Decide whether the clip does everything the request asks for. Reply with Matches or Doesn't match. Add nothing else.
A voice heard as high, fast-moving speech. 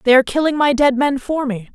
Matches